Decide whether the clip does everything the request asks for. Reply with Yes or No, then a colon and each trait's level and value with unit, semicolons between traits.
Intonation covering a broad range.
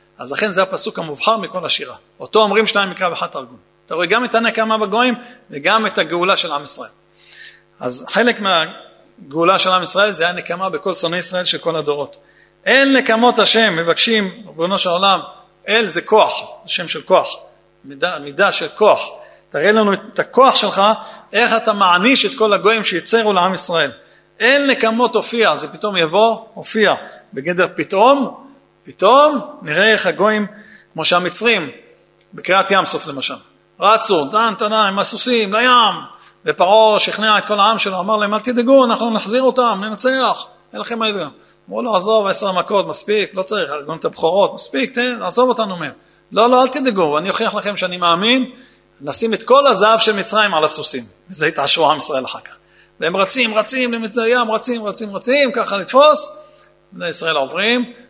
No: average, 4.0 semitones